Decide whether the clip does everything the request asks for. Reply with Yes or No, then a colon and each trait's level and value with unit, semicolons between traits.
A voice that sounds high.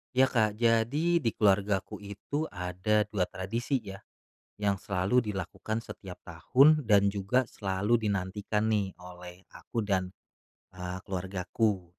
No: low, 100 Hz